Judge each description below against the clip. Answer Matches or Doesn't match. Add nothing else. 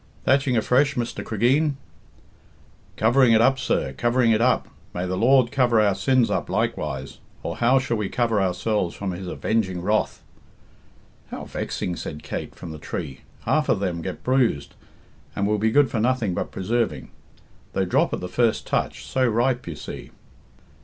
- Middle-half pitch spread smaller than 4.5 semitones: Doesn't match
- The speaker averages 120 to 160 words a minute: Doesn't match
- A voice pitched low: Matches